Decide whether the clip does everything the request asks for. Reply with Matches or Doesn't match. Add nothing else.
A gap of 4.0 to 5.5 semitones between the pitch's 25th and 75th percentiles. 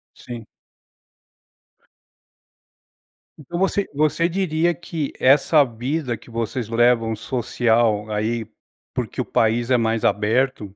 Matches